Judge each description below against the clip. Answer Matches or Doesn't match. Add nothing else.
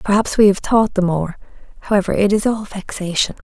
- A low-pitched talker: Doesn't match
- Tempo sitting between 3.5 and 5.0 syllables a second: Doesn't match